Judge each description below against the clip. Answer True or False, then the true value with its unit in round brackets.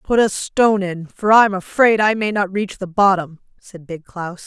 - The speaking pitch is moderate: False (195 Hz)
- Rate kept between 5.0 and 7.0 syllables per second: False (4.8 syllables/s)